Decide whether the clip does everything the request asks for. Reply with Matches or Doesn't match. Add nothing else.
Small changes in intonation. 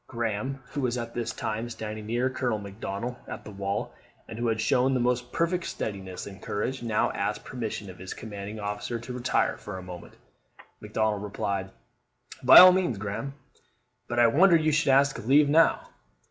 Doesn't match